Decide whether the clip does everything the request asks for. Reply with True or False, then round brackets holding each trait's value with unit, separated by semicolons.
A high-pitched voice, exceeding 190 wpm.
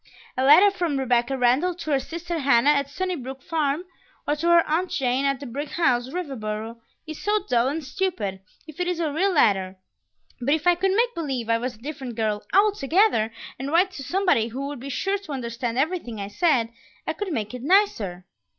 True (280 Hz; 205 wpm)